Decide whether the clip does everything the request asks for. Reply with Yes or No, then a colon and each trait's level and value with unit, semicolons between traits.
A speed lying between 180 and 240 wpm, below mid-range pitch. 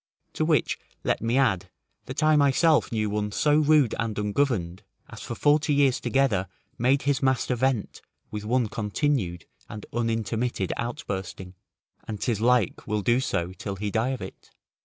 No: average, 160 wpm; low, 115 Hz